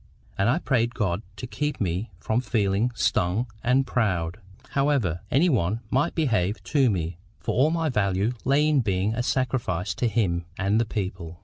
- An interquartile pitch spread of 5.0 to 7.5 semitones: Yes, wide, 5.6 semitones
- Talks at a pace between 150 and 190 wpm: Yes, average, 175 wpm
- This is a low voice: Yes, low, 110 Hz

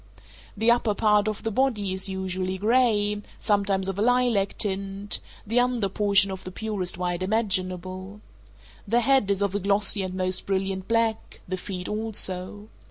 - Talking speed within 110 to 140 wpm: No, average, 165 wpm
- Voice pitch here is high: Yes, high, 200 Hz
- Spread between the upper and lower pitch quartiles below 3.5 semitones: Yes, narrow, 2.5 semitones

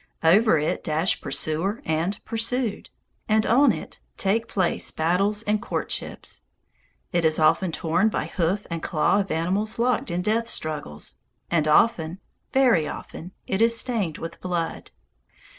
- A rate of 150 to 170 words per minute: No, average, 140 wpm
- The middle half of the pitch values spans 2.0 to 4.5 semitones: No, average, 5.1 semitones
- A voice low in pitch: No, medium, 185 Hz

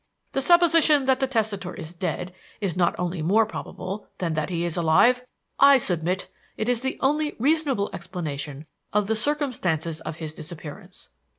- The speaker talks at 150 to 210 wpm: Yes, average, 165 wpm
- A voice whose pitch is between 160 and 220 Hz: Yes, high, 190 Hz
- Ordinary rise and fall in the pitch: No, wide, 7.8 semitones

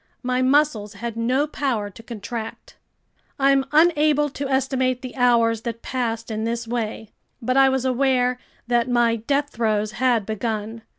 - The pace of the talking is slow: No, average, 155 wpm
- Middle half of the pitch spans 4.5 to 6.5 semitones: No, average, 2.7 semitones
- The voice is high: Yes, high, 245 Hz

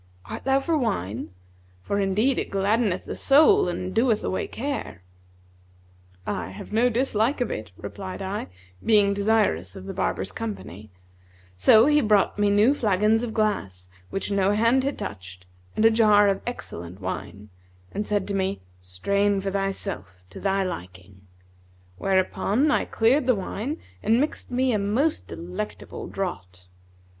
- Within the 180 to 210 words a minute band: No, average, 150 wpm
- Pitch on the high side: Yes, high, 200 Hz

